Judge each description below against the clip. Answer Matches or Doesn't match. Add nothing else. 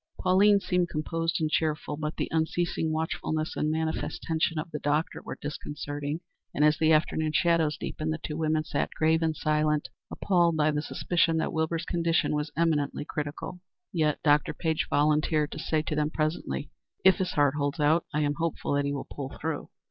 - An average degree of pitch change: Doesn't match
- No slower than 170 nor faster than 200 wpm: Matches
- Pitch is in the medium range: Matches